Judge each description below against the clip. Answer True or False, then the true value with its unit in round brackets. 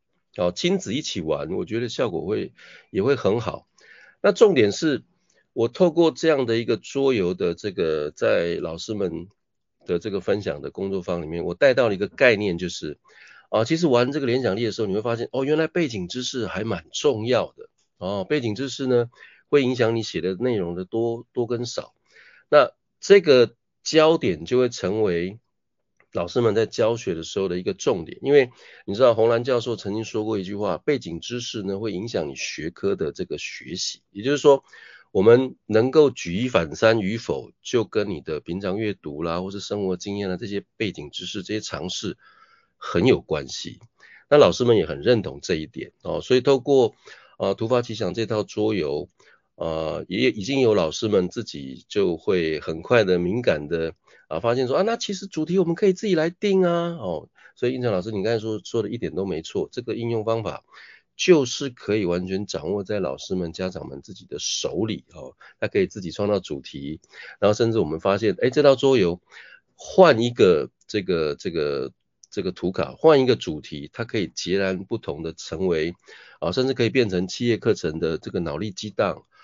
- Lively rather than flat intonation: True (6.5 semitones)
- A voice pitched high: False (115 Hz)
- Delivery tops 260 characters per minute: True (285 characters per minute)